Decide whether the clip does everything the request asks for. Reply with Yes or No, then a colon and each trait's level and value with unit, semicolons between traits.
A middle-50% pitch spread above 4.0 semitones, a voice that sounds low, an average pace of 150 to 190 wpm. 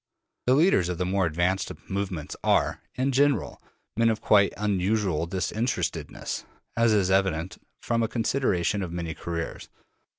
No: average, 4.5 semitones; very low, 95 Hz; average, 140 wpm